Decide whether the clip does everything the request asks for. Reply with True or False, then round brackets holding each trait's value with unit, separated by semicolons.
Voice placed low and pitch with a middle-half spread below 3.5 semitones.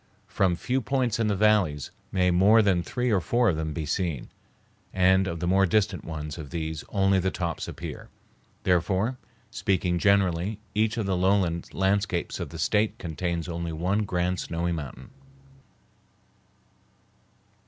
True (95 Hz; 3.1 semitones)